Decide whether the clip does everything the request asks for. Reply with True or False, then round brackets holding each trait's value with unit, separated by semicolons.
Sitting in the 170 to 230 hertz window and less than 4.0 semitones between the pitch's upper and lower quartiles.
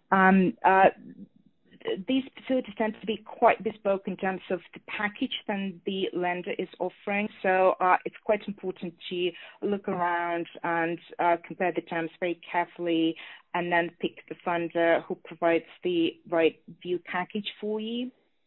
True (185 Hz; 3.6 semitones)